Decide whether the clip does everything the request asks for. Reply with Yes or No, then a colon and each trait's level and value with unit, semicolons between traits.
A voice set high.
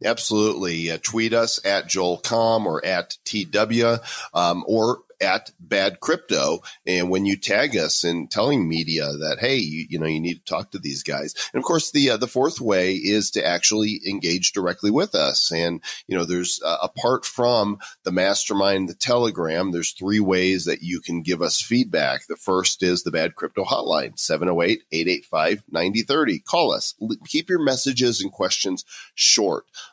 No: very low, 95 Hz